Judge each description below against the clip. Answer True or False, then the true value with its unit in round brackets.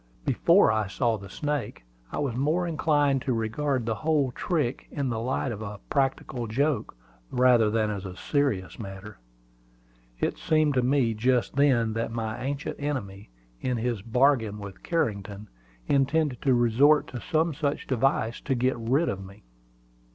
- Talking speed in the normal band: True (160 wpm)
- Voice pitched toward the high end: False (125 Hz)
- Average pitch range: True (4.5 semitones)